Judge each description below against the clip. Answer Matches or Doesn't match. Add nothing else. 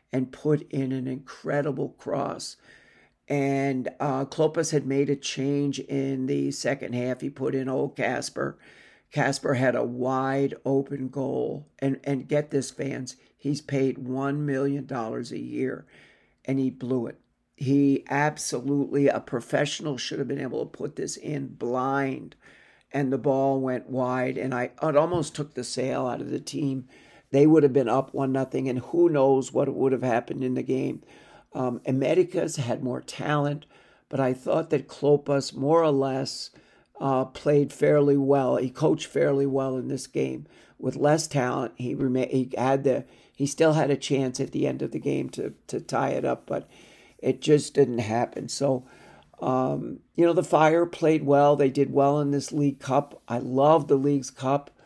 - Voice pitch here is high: Doesn't match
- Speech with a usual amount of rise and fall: Doesn't match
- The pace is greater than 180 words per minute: Doesn't match